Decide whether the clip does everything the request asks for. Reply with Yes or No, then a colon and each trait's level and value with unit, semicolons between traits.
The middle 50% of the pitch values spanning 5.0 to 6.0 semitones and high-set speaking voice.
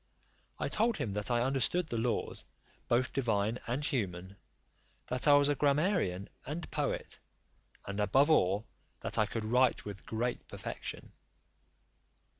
No: wide, 5.6 semitones; low, 120 Hz